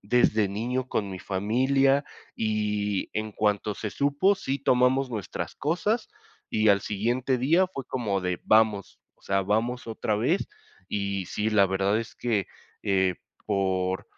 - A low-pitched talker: Yes, low, 110 Hz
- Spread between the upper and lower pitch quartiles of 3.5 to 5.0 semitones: Yes, average, 4.3 semitones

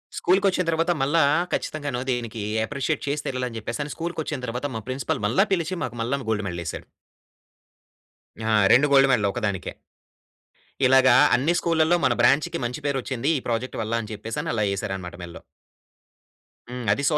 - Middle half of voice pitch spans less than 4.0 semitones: No, average, 4.5 semitones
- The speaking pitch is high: No, low, 130 Hz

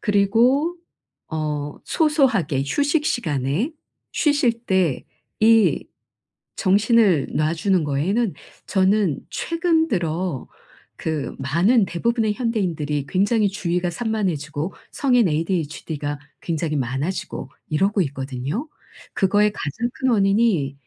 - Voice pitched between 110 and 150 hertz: No, high, 190 Hz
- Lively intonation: Yes, wide, 7.1 semitones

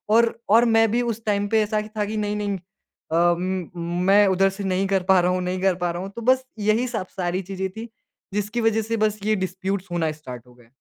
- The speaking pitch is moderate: No, high, 195 Hz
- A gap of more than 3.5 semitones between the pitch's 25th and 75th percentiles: No, average, 2.8 semitones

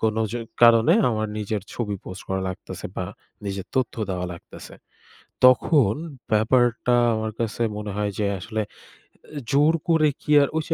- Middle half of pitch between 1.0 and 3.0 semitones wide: No, average, 3.8 semitones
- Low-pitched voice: Yes, low, 110 Hz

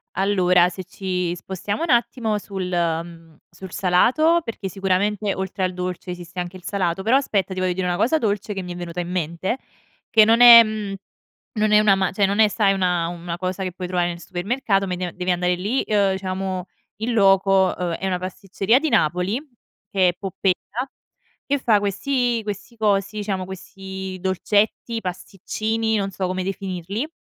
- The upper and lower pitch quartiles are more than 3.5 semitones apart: No, average, 2.8 semitones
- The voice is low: No, high, 190 Hz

